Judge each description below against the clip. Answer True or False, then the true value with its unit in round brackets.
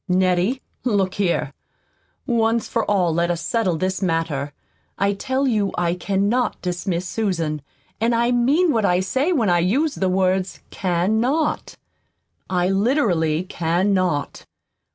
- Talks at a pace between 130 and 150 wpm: True (140 wpm)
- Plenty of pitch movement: False (4.7 semitones)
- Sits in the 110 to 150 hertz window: False (190 Hz)